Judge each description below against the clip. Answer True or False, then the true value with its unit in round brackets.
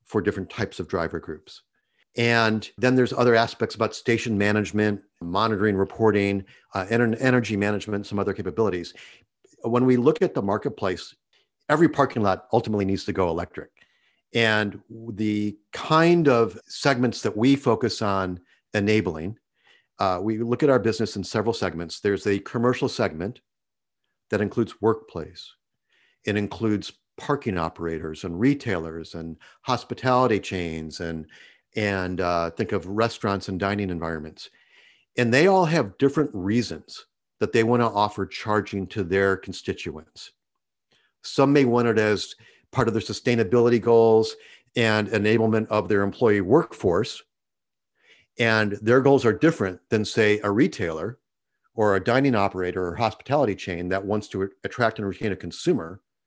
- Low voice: True (105 Hz)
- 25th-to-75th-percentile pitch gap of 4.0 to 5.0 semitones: False (3.3 semitones)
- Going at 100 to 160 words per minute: True (145 wpm)